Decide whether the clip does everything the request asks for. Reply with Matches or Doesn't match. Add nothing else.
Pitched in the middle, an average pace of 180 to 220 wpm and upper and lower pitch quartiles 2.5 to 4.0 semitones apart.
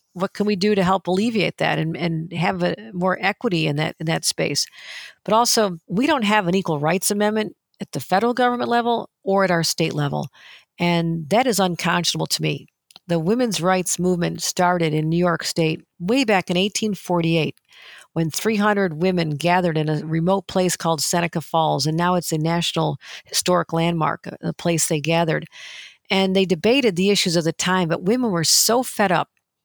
Matches